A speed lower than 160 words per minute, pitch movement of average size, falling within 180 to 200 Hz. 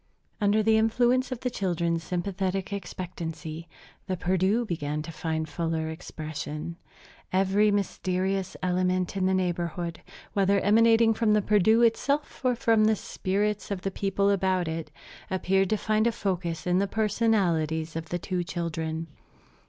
Yes: average, 145 wpm; average, 3.8 semitones; high, 190 Hz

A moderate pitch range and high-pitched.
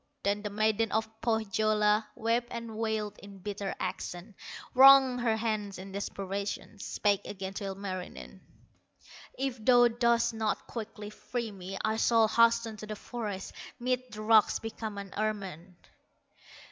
No: narrow, 2.3 semitones; high, 215 Hz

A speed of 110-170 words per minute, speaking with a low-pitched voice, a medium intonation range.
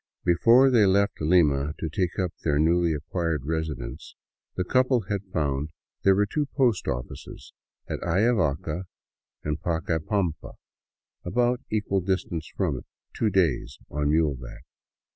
Yes: average, 140 wpm; very low, 85 Hz; average, 4.8 semitones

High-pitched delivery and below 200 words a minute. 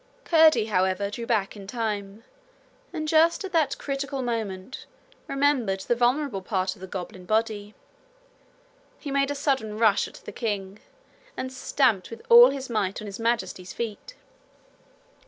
Yes: high, 230 Hz; average, 150 wpm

